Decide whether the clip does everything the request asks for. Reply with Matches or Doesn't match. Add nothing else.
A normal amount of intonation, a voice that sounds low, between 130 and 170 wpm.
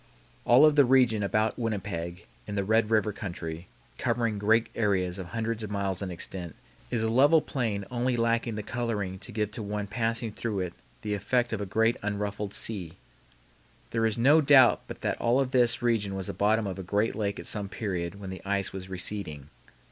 Doesn't match